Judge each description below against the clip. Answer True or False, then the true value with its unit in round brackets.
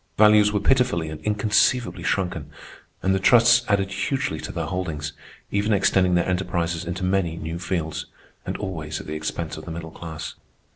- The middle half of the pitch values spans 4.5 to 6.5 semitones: False (4.0 semitones)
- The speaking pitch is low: True (90 Hz)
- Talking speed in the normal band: True (165 wpm)